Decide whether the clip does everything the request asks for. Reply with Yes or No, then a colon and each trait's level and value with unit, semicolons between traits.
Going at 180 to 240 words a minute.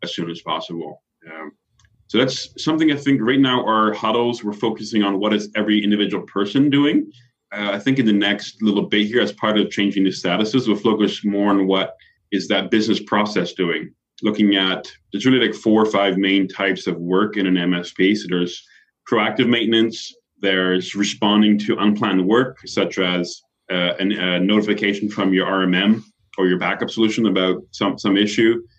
Yes: average, 185 wpm